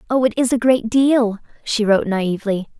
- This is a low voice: No, high, 230 Hz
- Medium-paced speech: Yes, average, 195 wpm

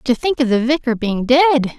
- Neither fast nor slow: No, fast, 235 wpm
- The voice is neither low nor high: No, very high, 250 Hz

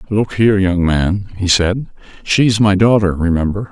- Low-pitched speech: Yes, low, 100 Hz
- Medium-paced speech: Yes, average, 180 wpm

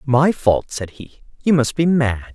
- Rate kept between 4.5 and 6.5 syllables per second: No, 4.2 syllables/s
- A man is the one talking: Yes, male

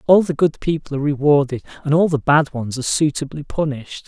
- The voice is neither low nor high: Yes, medium, 145 Hz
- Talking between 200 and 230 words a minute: Yes, fast, 205 wpm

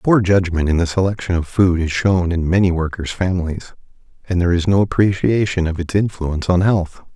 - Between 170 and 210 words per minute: Yes, average, 195 wpm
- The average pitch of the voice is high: No, very low, 90 Hz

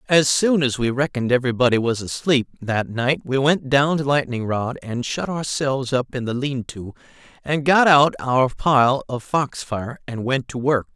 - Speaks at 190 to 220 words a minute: Yes, average, 195 wpm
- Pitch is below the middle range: Yes, low, 130 Hz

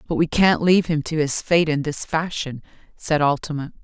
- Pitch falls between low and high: Yes, medium, 155 Hz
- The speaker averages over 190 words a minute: Yes, fast, 205 wpm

